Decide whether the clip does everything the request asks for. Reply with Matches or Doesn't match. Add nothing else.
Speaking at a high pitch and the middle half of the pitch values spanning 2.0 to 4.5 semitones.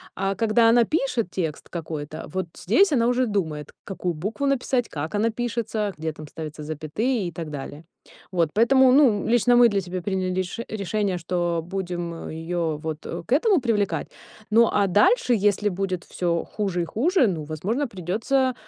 Doesn't match